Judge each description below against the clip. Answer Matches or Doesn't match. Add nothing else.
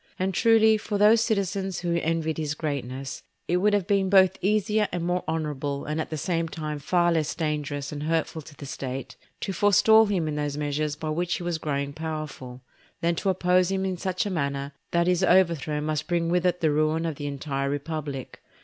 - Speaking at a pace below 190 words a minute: Doesn't match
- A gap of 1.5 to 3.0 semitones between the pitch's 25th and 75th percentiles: Doesn't match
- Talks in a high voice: Doesn't match